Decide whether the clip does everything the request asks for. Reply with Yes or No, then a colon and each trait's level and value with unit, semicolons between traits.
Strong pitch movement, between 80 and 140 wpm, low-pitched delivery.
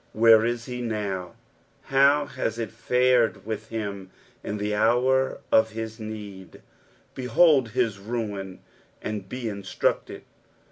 No: average, 3.0 semitones; slow, 135 wpm; low, 110 Hz